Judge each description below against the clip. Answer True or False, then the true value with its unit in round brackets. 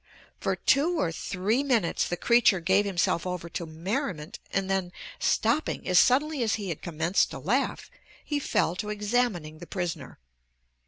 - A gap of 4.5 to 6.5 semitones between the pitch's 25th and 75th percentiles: True (5.6 semitones)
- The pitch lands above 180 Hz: True (190 Hz)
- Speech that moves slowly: False (160 wpm)